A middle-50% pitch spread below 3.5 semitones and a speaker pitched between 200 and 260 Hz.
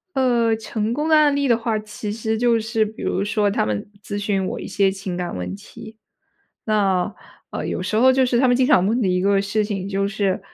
Yes: average, 3.0 semitones; high, 215 Hz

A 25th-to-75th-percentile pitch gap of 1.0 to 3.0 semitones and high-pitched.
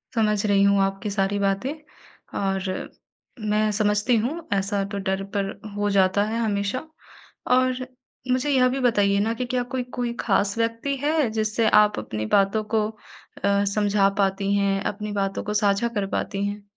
Yes: narrow, 2.6 semitones; high, 205 Hz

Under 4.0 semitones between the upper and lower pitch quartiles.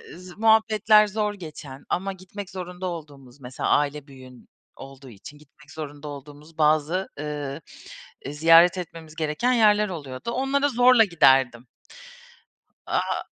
No: wide, 5.5 semitones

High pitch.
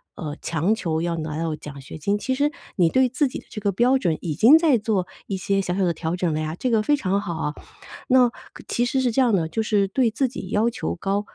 Yes: high, 200 Hz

